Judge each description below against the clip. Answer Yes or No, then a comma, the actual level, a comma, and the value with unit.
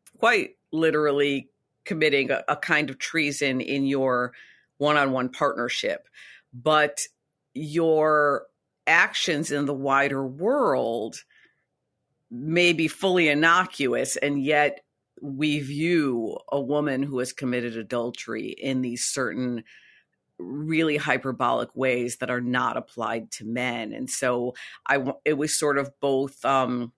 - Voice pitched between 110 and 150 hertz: Yes, medium, 140 Hz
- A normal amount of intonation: Yes, average, 3.0 semitones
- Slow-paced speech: Yes, slow, 120 wpm